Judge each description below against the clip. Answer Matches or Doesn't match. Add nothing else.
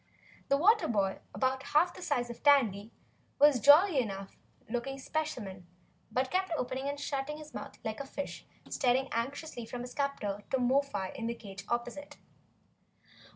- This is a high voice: Matches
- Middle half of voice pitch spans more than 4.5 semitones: Doesn't match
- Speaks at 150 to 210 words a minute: Matches